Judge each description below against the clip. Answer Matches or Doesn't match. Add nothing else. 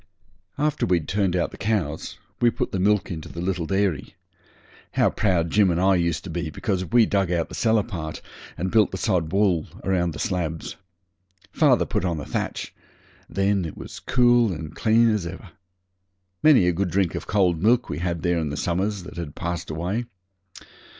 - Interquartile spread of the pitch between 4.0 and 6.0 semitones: Doesn't match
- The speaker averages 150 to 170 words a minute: Doesn't match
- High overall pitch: Doesn't match